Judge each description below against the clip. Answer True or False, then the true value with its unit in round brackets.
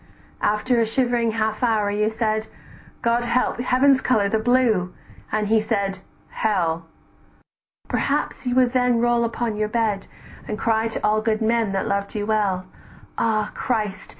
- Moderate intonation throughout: False (2.1 semitones)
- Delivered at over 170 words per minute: False (155 wpm)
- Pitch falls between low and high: False (220 Hz)